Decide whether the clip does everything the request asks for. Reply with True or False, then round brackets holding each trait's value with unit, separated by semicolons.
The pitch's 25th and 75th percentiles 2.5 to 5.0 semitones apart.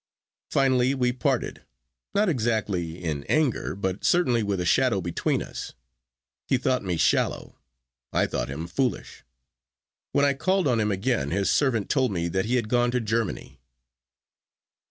False (5.5 semitones)